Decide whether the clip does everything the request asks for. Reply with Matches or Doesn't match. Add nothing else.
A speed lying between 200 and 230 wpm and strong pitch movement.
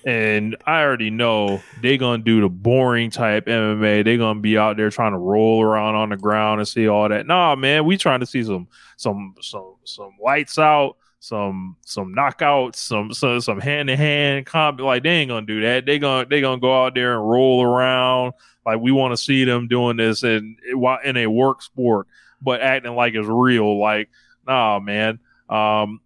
Doesn't match